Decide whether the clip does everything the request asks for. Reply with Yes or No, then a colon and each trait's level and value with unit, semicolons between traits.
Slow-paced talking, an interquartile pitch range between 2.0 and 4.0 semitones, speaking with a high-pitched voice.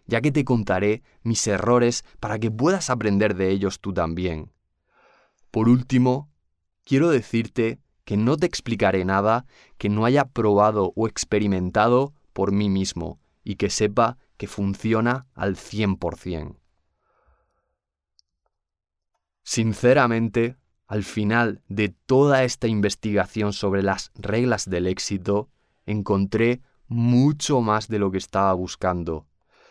No: slow, 120 wpm; average, 3.6 semitones; low, 105 Hz